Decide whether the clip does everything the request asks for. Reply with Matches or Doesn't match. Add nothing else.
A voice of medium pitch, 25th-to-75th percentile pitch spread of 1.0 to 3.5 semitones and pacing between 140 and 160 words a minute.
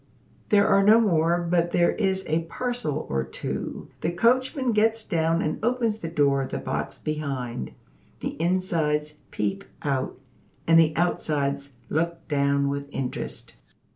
Doesn't match